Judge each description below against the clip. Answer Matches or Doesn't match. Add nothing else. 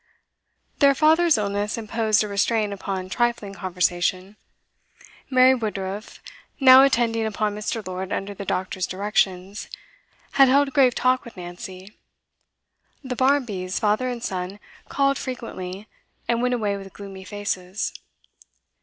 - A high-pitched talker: Matches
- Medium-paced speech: Doesn't match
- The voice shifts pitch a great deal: Doesn't match